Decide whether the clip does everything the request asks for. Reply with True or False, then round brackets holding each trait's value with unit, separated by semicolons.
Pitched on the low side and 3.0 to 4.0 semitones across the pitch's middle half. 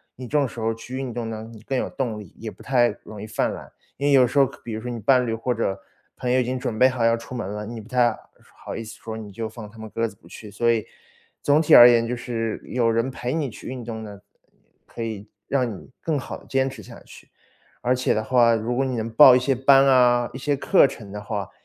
False (120 Hz; 2.5 semitones)